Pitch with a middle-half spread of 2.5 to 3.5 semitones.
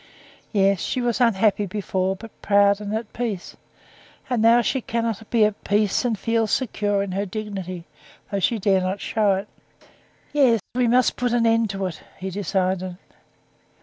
Yes: average, 3.0 semitones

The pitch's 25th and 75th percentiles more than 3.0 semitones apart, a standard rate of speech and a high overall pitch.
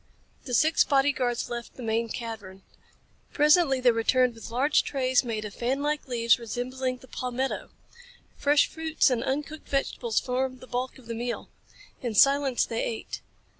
No: average, 2.7 semitones; average, 160 wpm; very high, 255 Hz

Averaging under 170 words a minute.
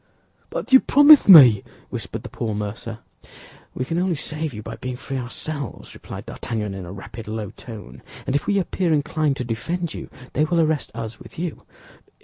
No: average, 185 wpm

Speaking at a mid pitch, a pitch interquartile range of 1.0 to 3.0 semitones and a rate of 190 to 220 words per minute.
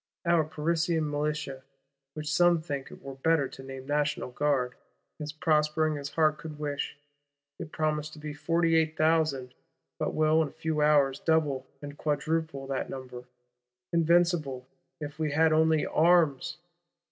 No: medium, 150 Hz; narrow, 2.4 semitones; average, 140 wpm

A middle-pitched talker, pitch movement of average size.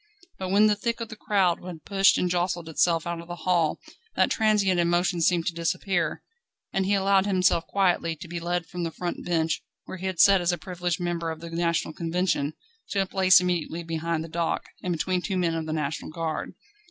No: medium, 175 Hz; narrow, 2.1 semitones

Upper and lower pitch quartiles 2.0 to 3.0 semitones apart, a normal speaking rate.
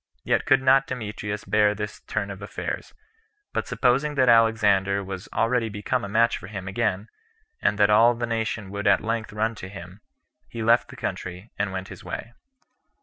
Yes: average, 2.7 semitones; average, 185 wpm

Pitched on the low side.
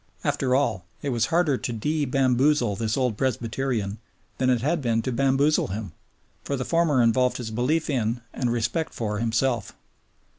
Yes: low, 125 Hz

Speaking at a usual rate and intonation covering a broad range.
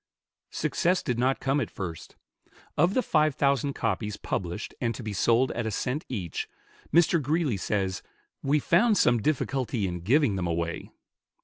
Yes: average, 165 wpm; wide, 6.6 semitones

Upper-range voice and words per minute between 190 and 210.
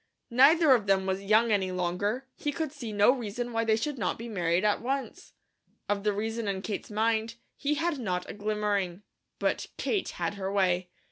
Yes: high, 215 Hz; average, 195 wpm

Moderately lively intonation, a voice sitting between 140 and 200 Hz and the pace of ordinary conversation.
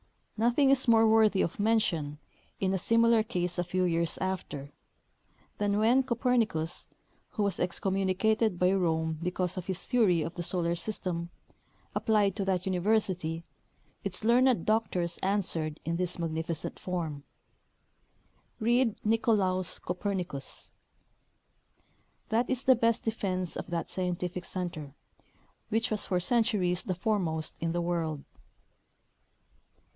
No: average, 4.2 semitones; medium, 185 Hz; slow, 130 wpm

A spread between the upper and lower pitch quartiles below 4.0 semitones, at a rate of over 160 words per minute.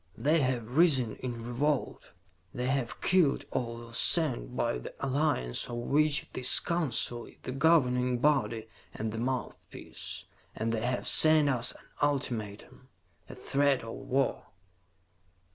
No: average, 3.5 semitones; average, 140 wpm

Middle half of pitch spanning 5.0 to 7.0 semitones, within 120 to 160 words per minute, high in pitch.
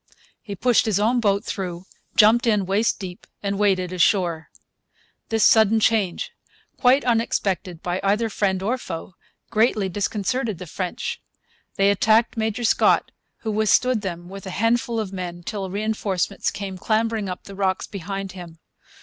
No: average, 3.0 semitones; average, 150 wpm; high, 200 Hz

